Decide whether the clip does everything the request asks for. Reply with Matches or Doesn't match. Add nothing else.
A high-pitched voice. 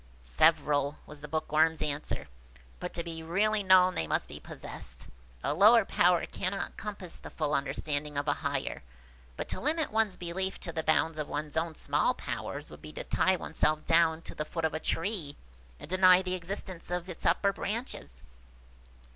Doesn't match